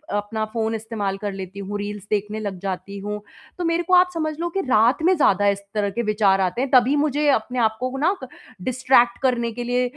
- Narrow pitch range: No, average, 4.5 semitones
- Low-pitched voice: No, high, 225 Hz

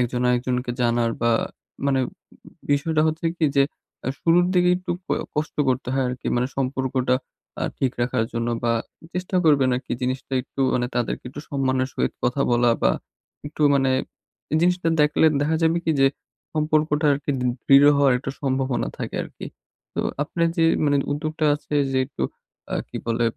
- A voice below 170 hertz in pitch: Yes, low, 135 Hz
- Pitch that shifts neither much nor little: Yes, average, 3.5 semitones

